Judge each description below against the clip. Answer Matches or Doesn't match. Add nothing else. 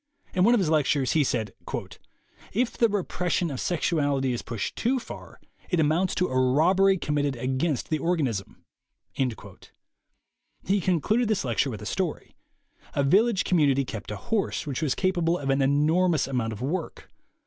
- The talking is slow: Doesn't match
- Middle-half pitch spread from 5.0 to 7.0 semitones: Matches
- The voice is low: Doesn't match